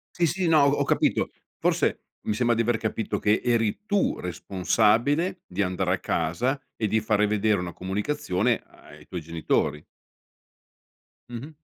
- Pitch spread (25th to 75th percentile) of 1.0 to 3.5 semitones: No, wide, 5.8 semitones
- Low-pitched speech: Yes, low, 110 Hz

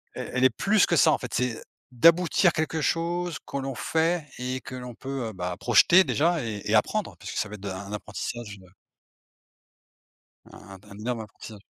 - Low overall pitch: Yes, low, 125 Hz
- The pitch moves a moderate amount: No, wide, 7.4 semitones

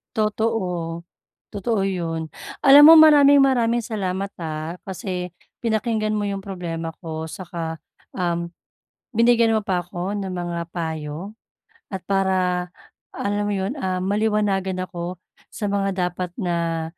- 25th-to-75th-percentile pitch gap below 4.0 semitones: Yes, average, 3.5 semitones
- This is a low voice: No, high, 190 Hz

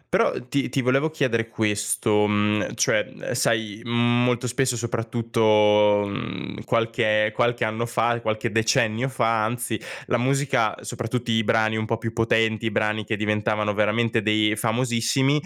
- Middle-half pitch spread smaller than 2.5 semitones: Yes, narrow, 2.0 semitones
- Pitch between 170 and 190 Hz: No, low, 115 Hz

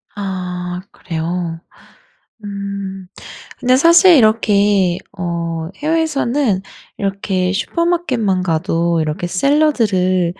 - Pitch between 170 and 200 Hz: Yes, high, 195 Hz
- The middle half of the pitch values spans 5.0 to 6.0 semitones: Yes, wide, 5.5 semitones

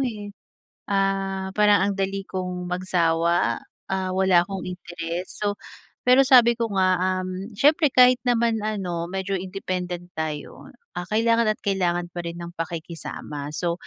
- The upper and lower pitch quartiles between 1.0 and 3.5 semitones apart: Yes, average, 2.8 semitones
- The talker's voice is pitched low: No, high, 190 Hz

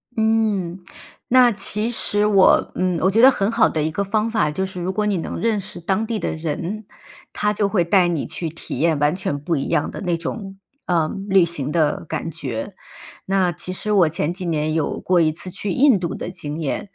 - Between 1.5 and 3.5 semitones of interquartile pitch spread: No, average, 4.1 semitones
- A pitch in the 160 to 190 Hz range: Yes, medium, 185 Hz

